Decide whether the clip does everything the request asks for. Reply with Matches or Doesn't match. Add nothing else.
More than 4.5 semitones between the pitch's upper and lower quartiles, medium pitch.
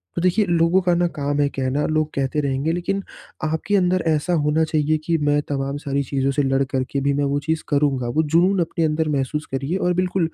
Doesn't match